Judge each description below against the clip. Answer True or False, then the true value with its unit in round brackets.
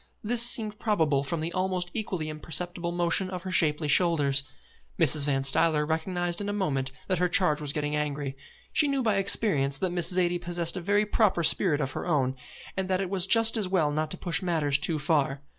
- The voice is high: False (170 Hz)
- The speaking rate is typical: False (210 wpm)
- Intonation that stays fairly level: False (4.1 semitones)